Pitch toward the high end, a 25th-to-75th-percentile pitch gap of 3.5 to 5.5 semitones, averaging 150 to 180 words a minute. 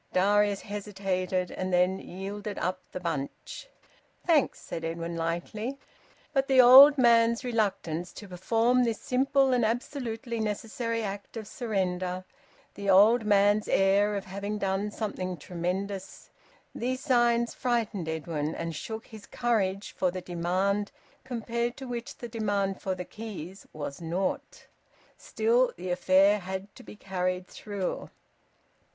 No: high, 200 Hz; average, 3.9 semitones; slow, 135 wpm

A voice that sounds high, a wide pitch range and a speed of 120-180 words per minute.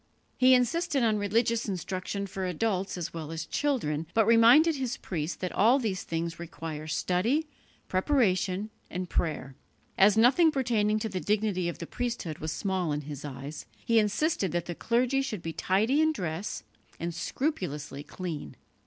Yes: high, 195 Hz; wide, 5.9 semitones; average, 160 wpm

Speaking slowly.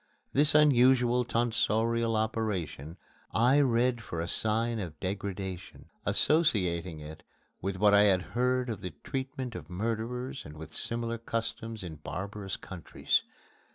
Yes: slow, 130 wpm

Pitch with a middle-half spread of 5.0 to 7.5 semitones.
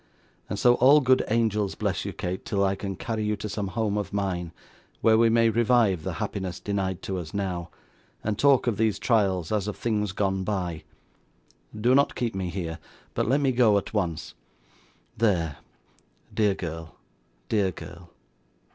No: average, 3.3 semitones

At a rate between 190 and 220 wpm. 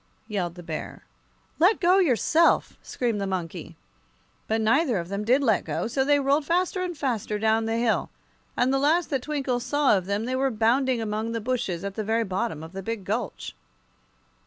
Yes: average, 195 wpm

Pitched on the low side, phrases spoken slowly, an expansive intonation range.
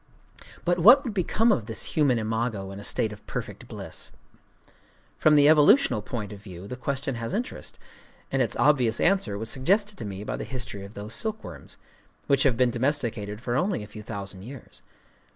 No: low, 120 Hz; average, 185 wpm; wide, 6.2 semitones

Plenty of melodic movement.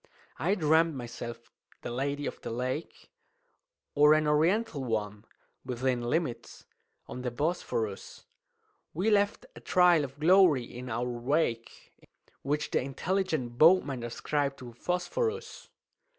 Yes: wide, 5.9 semitones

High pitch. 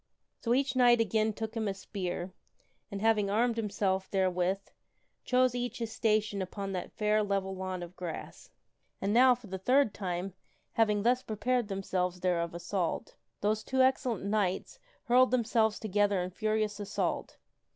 Yes: high, 210 Hz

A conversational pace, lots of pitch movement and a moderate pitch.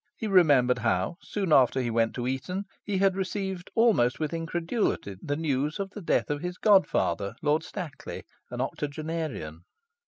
Yes: average, 165 wpm; wide, 7.0 semitones; medium, 155 Hz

